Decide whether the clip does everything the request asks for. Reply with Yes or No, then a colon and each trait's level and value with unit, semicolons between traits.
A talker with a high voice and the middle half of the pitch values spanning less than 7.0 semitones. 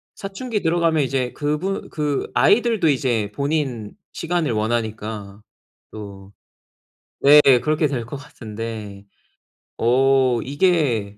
No: low, 135 Hz; wide, 6.1 semitones